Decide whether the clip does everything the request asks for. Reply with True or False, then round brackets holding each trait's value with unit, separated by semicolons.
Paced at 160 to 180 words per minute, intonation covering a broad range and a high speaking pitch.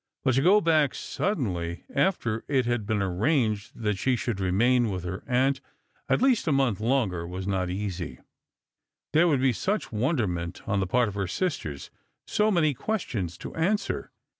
False (170 wpm; 7.1 semitones; 120 Hz)